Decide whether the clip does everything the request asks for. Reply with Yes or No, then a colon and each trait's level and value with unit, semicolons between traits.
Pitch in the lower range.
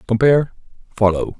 Yes: low, 115 Hz